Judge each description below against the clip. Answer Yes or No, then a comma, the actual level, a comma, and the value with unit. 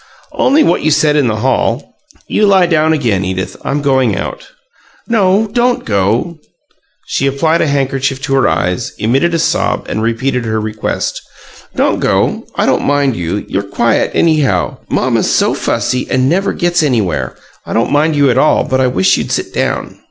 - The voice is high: No, low, 135 Hz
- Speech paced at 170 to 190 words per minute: Yes, average, 180 wpm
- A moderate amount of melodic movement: No, wide, 6.1 semitones